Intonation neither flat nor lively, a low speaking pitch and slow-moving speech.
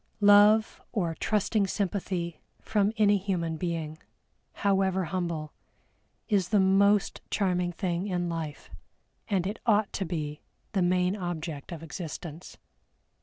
No: average, 3.0 semitones; medium, 180 Hz; slow, 120 wpm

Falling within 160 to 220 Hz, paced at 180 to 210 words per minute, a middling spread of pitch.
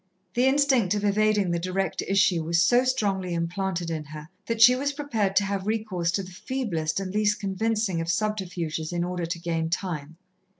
Yes: high, 190 Hz; average, 185 wpm; average, 3.9 semitones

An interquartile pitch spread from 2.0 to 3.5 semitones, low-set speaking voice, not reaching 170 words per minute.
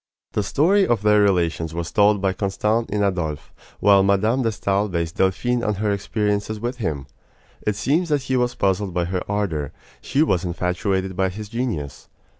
No: average, 3.2 semitones; low, 100 Hz; average, 180 wpm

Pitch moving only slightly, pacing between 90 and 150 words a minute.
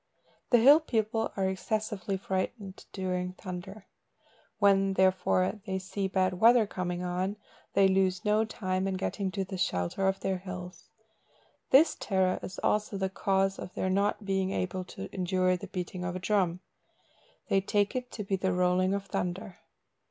No: narrow, 1.6 semitones; average, 165 wpm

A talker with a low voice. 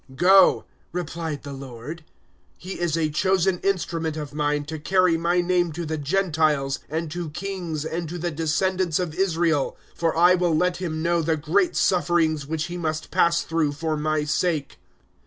No: medium, 165 Hz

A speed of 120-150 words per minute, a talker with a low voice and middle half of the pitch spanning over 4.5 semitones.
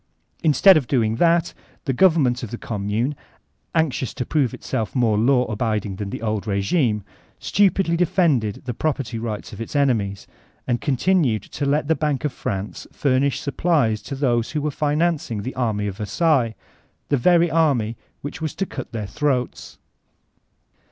No: average, 160 wpm; low, 130 Hz; wide, 5.6 semitones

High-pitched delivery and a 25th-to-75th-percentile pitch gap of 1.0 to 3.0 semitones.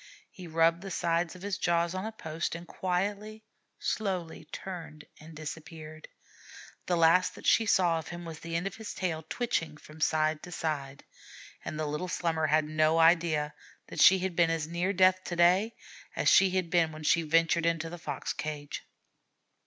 No: medium, 165 Hz; average, 2.7 semitones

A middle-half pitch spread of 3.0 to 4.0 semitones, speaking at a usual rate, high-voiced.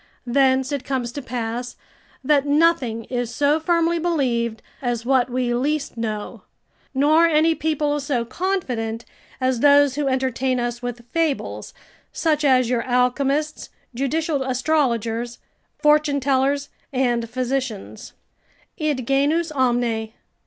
No: average, 3.5 semitones; slow, 120 wpm; very high, 265 Hz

